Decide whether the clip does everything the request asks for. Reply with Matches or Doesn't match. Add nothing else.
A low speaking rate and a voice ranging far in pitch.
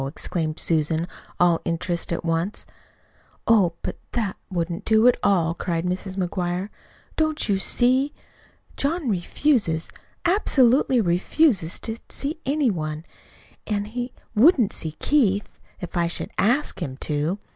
Matches